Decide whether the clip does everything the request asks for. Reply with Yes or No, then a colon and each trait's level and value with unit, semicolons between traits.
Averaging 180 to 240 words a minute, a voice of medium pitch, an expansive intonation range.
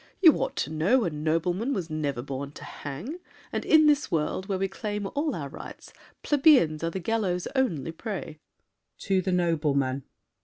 No: average, 170 wpm; medium, 180 Hz; wide, 6.5 semitones